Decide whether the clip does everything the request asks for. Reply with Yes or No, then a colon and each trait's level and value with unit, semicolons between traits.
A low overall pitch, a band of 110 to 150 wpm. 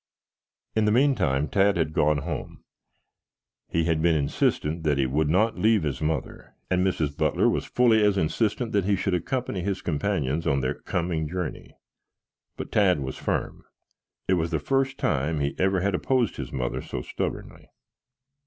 No: very low, 85 Hz; average, 170 wpm